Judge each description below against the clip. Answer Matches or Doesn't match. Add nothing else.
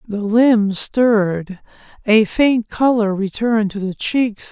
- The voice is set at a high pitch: Matches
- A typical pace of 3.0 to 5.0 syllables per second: Matches